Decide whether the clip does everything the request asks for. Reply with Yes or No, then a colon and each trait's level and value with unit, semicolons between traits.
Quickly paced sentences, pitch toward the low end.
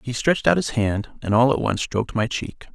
Yes: fast, 260 wpm; low, 115 Hz